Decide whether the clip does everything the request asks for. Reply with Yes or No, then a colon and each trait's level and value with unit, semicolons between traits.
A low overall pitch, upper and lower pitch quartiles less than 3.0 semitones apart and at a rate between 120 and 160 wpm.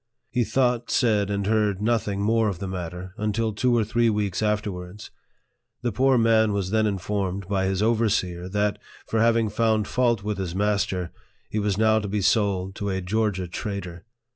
No: low, 105 Hz; narrow, 2.5 semitones; average, 190 wpm